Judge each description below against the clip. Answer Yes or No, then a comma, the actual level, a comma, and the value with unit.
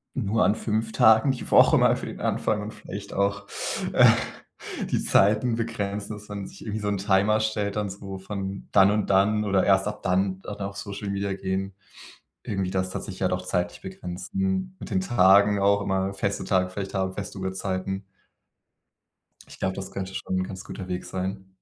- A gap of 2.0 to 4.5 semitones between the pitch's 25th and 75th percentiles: No, narrow, 1.6 semitones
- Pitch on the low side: Yes, low, 100 Hz